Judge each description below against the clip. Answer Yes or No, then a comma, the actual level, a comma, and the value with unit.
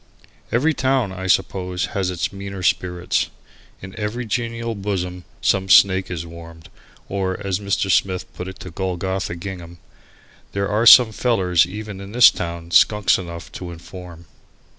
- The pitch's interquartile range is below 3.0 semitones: Yes, narrow, 2.4 semitones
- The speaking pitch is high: No, very low, 95 Hz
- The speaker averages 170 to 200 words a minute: No, average, 150 wpm